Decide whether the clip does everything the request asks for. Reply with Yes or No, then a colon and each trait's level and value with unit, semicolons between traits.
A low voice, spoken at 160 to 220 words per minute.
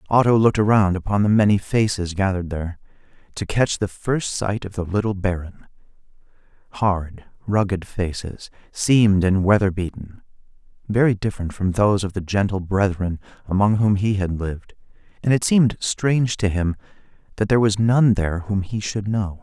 Yes: low, 100 Hz; average, 165 wpm